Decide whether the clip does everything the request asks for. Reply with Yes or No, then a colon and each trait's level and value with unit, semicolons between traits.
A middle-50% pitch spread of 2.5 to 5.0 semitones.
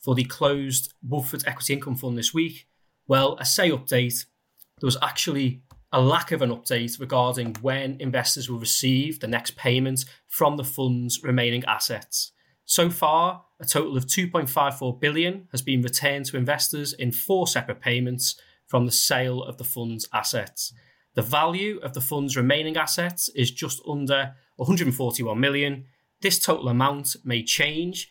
Yes: average, 2.9 semitones